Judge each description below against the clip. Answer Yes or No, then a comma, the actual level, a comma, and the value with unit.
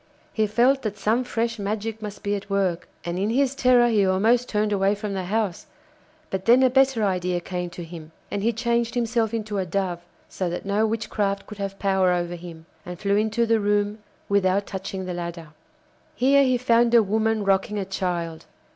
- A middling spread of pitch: Yes, average, 3.4 semitones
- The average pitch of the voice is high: Yes, high, 205 Hz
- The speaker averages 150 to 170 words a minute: No, average, 200 wpm